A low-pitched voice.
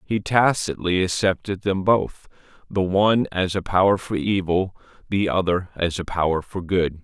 Yes: very low, 95 Hz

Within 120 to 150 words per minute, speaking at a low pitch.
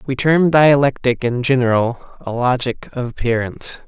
Yes: average, 140 wpm; low, 125 Hz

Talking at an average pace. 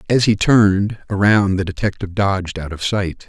Yes: average, 185 wpm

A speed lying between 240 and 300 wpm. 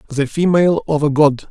No: average, 200 wpm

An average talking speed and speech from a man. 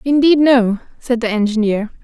No: average, 150 wpm; female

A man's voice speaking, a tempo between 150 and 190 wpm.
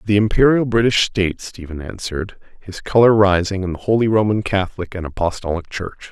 Yes: male; average, 165 wpm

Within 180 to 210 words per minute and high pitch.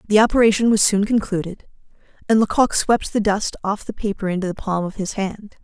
Yes: average, 200 wpm; high, 205 Hz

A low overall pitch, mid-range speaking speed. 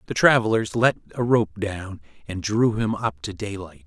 Yes: low, 105 Hz; average, 185 wpm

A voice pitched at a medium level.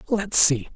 Yes: medium, 165 Hz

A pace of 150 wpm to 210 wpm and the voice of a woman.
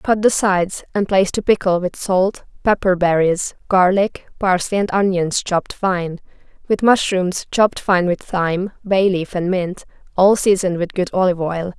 Yes: average, 170 wpm; female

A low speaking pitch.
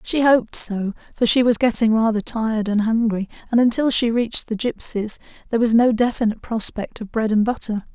No: high, 225 Hz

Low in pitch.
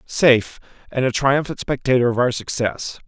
Yes: low, 130 Hz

